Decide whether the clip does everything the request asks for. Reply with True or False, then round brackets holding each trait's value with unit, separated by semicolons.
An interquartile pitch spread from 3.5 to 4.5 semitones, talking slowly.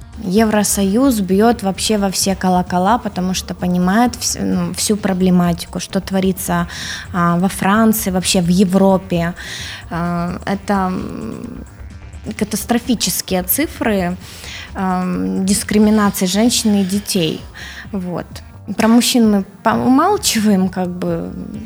False (3.0 semitones; 90 wpm)